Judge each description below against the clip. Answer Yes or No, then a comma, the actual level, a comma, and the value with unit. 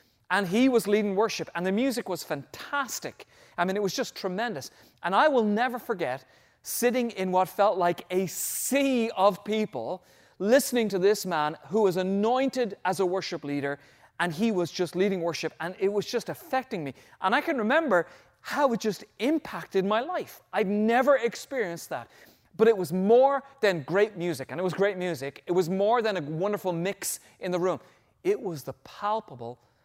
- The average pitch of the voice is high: Yes, high, 200 Hz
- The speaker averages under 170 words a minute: No, average, 185 wpm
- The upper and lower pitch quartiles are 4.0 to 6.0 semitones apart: Yes, average, 4.8 semitones